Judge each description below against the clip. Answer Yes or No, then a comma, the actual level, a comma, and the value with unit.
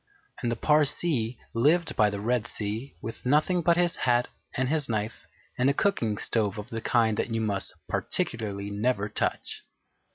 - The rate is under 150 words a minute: No, average, 170 wpm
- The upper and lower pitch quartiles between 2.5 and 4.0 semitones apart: No, average, 4.7 semitones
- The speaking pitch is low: Yes, low, 115 Hz